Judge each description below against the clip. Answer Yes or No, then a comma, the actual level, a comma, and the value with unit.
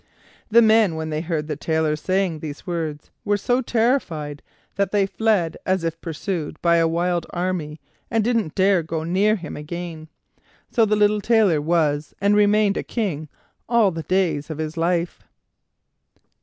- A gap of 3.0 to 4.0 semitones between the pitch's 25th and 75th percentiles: No, average, 4.5 semitones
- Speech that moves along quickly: No, average, 165 wpm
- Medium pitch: Yes, medium, 175 Hz